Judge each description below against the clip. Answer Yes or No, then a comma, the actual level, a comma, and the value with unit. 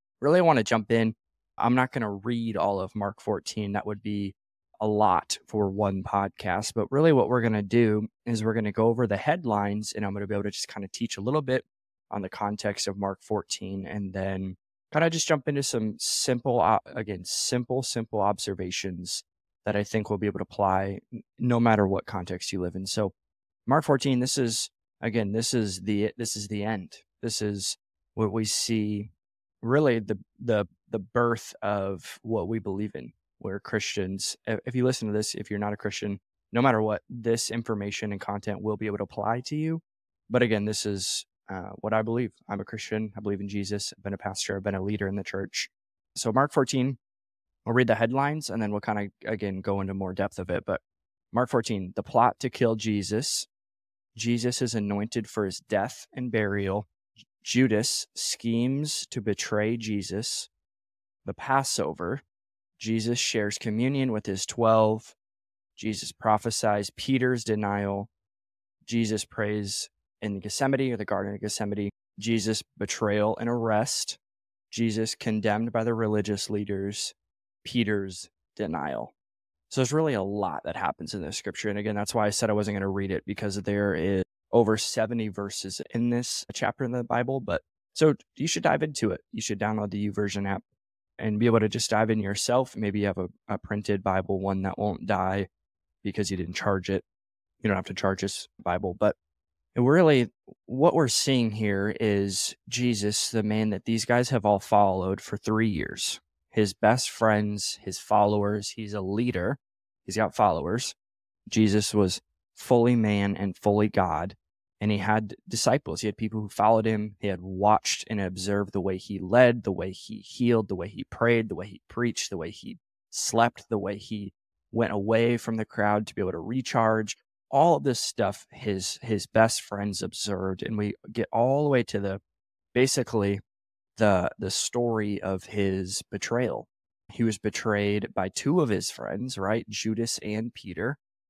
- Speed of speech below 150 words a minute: No, average, 185 wpm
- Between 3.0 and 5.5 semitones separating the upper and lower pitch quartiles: No, narrow, 2.5 semitones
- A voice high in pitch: No, low, 105 Hz